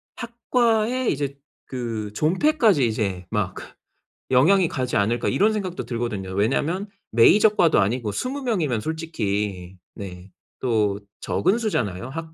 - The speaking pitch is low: Yes, low, 130 Hz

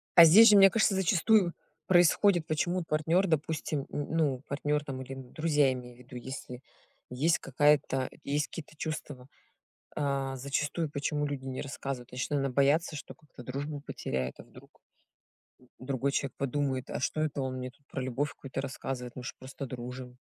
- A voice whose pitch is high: No, medium, 140 Hz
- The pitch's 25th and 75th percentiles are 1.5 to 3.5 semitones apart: Yes, average, 3.1 semitones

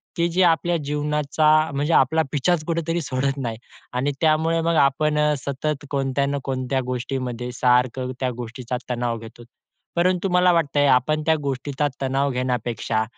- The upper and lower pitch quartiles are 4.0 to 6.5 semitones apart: No, average, 3.4 semitones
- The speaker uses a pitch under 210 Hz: Yes, medium, 140 Hz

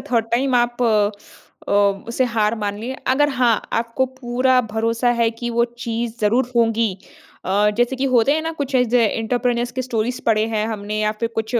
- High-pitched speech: Yes, high, 235 Hz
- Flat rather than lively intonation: Yes, narrow, 2.1 semitones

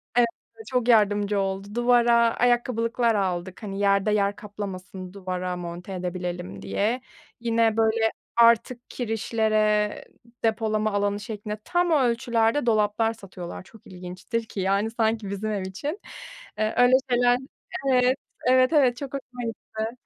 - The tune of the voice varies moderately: Yes, average, 3.2 semitones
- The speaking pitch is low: No, high, 220 Hz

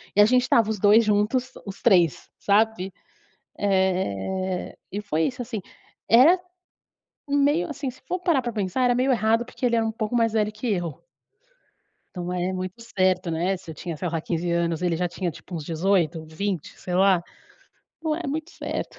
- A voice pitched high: Yes, high, 200 Hz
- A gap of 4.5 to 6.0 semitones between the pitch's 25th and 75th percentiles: Yes, average, 4.9 semitones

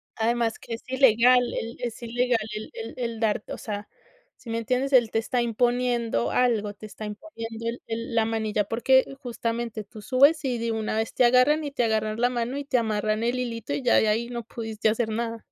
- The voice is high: Yes, high, 230 Hz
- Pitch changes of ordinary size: No, narrow, 2.0 semitones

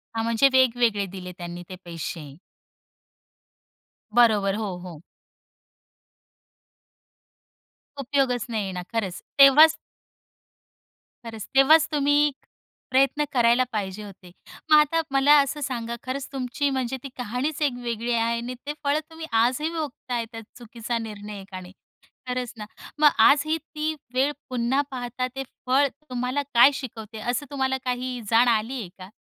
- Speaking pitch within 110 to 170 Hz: No, high, 245 Hz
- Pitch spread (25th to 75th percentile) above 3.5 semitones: Yes, average, 3.9 semitones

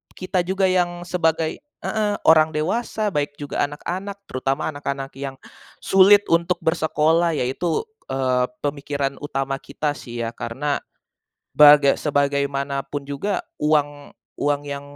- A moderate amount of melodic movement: Yes, average, 3.8 semitones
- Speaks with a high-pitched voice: No, medium, 145 Hz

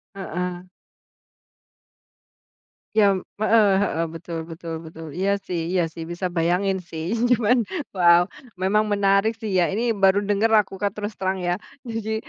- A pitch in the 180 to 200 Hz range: Yes, high, 190 Hz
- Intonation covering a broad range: No, average, 3.0 semitones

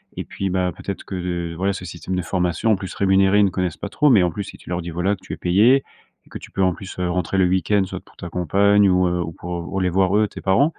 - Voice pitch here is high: No, very low, 95 Hz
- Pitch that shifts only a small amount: Yes, narrow, 1.9 semitones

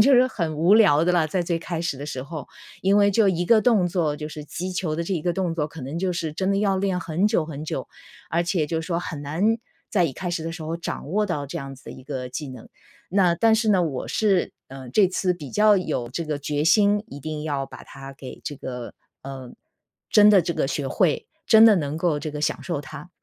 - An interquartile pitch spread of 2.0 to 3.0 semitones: No, average, 4.4 semitones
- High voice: No, medium, 165 Hz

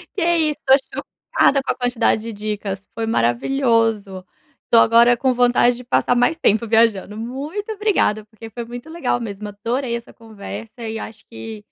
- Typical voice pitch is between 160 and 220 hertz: No, high, 230 Hz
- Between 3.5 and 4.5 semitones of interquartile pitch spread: No, average, 2.9 semitones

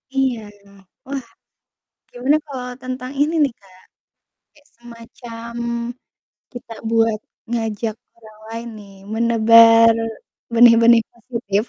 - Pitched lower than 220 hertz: No, high, 230 Hz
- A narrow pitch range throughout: Yes, narrow, 1.6 semitones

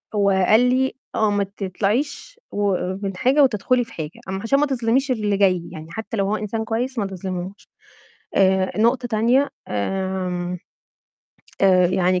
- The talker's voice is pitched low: No, high, 205 Hz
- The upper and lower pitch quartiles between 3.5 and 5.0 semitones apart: Yes, average, 4.2 semitones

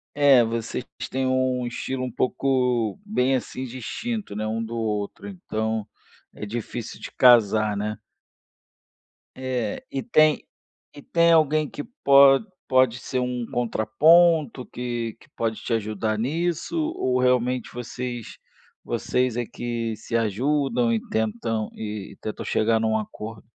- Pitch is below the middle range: Yes, low, 120 Hz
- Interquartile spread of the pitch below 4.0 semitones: Yes, average, 3.1 semitones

